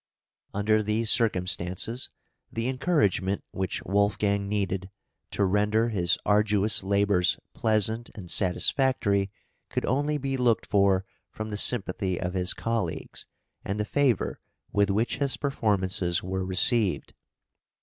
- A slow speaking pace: Yes, slow, 120 wpm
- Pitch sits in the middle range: No, low, 105 Hz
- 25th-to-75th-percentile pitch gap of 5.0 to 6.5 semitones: No, average, 3.2 semitones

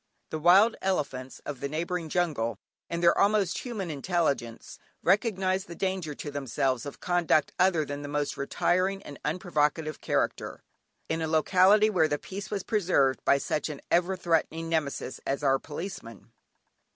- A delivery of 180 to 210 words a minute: No, average, 155 wpm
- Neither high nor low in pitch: Yes, medium, 165 Hz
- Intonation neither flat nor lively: Yes, average, 4.4 semitones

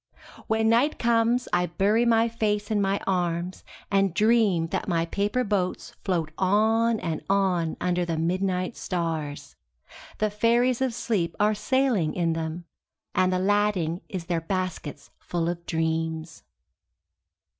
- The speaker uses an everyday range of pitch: Yes, average, 4.5 semitones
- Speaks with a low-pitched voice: No, medium, 185 Hz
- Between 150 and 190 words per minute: No, average, 140 wpm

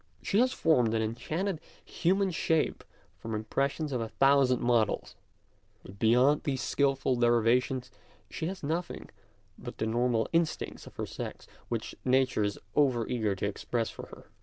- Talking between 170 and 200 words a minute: No, average, 155 wpm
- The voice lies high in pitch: No, low, 125 Hz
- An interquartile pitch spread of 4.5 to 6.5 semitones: Yes, average, 4.8 semitones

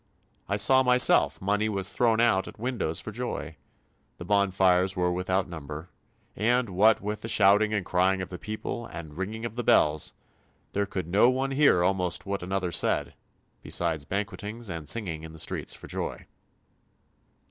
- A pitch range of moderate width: Yes, average, 3.5 semitones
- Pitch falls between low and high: No, low, 100 Hz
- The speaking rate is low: No, average, 165 wpm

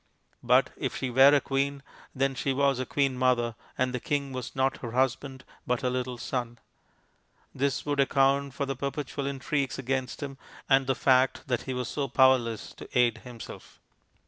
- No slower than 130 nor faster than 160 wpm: No, average, 180 wpm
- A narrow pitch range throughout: Yes, narrow, 1.6 semitones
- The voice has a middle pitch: No, low, 130 Hz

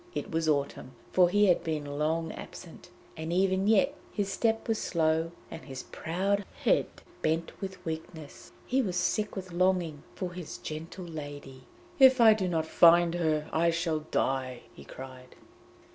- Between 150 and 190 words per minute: Yes, average, 160 wpm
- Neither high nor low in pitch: Yes, medium, 165 Hz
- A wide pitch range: No, average, 3.5 semitones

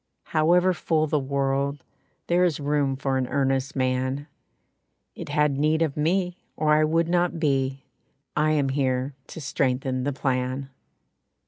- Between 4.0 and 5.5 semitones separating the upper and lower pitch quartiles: No, average, 2.7 semitones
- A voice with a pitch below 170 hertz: Yes, medium, 140 Hz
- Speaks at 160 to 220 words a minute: No, average, 145 wpm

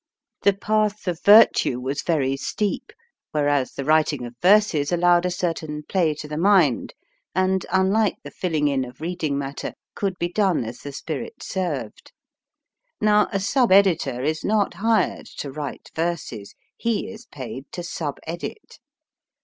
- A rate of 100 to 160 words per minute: Yes, average, 155 wpm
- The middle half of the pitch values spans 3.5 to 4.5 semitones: No, wide, 5.4 semitones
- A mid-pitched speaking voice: Yes, medium, 170 Hz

